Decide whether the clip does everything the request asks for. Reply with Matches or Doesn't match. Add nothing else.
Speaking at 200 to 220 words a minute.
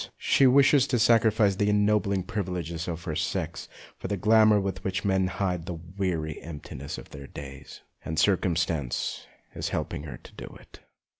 Doesn't match